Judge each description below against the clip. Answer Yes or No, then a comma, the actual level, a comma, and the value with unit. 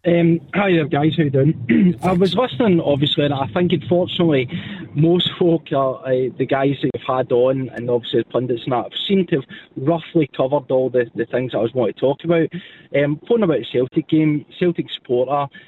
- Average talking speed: No, fast, 215 wpm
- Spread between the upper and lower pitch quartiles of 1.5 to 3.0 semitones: No, average, 4.7 semitones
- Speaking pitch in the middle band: Yes, medium, 150 Hz